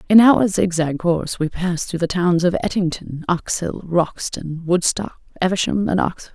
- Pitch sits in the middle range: Yes, medium, 175 Hz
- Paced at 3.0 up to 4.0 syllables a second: No, 4.8 syllables/s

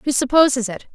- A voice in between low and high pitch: No, very high, 255 Hz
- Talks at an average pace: Yes, average, 190 wpm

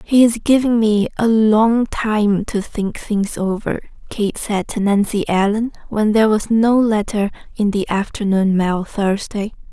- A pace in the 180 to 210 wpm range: No, average, 160 wpm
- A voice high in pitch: Yes, high, 210 Hz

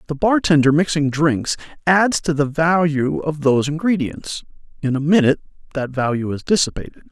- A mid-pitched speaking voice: Yes, medium, 155 Hz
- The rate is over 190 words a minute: No, average, 150 wpm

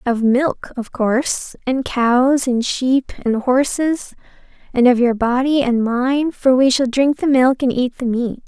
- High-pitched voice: Yes, very high, 255 Hz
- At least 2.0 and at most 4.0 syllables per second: Yes, 3.9 syllables/s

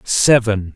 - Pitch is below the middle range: Yes, low, 110 Hz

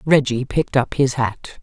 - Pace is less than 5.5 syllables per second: Yes, 4.6 syllables/s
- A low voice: Yes, low, 130 Hz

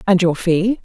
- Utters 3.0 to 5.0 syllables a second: Yes, 4.4 syllables/s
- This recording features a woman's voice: Yes, female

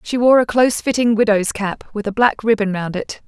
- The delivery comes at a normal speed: No, fast, 240 wpm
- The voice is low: No, high, 220 Hz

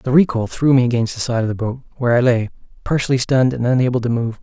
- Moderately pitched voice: No, low, 125 Hz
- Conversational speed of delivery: No, fast, 260 wpm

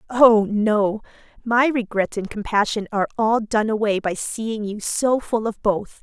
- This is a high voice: Yes, high, 215 Hz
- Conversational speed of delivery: Yes, average, 170 wpm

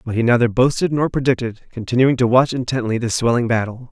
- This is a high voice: No, low, 120 Hz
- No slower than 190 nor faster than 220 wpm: Yes, average, 200 wpm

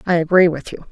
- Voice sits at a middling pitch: Yes, medium, 170 Hz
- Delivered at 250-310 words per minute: Yes, fast, 260 wpm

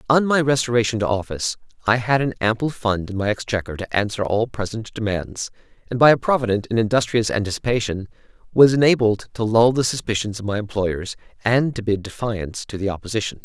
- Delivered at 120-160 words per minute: No, average, 185 wpm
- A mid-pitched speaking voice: No, low, 110 Hz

